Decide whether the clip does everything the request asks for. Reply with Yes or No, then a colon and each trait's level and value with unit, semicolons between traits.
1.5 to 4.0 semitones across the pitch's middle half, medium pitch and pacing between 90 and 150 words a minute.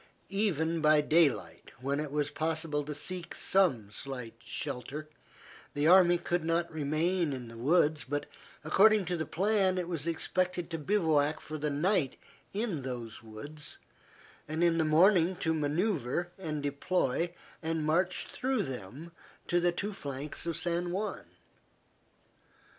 Yes: average, 3.5 semitones; medium, 160 Hz; average, 145 wpm